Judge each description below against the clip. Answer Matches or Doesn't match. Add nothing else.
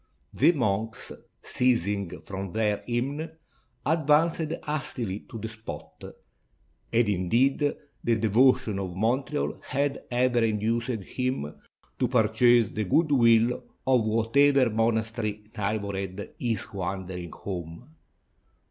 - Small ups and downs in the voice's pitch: Doesn't match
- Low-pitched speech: Matches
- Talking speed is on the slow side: Matches